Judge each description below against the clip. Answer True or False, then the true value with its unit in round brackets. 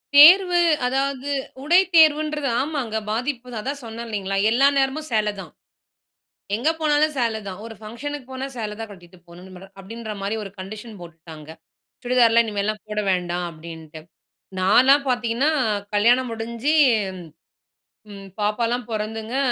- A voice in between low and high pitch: False (230 Hz)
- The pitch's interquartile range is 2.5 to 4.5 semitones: False (4.9 semitones)